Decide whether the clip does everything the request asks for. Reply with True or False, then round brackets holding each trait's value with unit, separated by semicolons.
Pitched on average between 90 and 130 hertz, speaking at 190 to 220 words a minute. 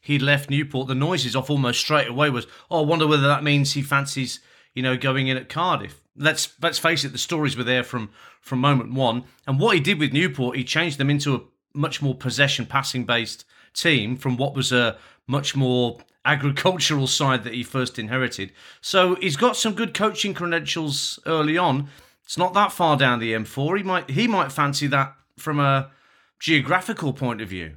False (140 Hz; 200 wpm)